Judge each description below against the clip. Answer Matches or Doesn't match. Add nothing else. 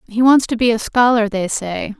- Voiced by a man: Doesn't match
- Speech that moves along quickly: Matches